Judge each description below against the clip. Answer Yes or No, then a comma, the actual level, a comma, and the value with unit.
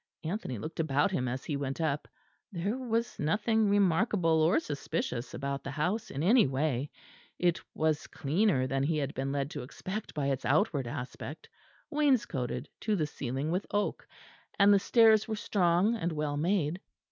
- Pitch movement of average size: No, wide, 6.6 semitones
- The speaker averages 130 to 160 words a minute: No, average, 170 wpm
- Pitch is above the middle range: No, medium, 160 Hz